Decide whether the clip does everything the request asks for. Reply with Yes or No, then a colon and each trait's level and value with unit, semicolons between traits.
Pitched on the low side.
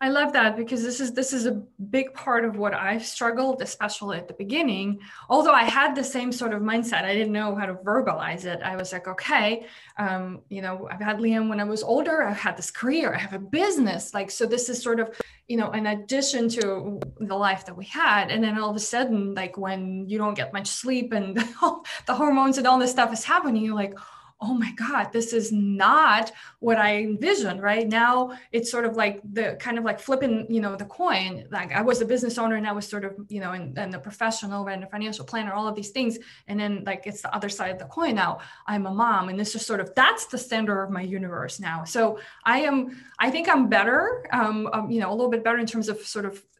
No: high, 220 Hz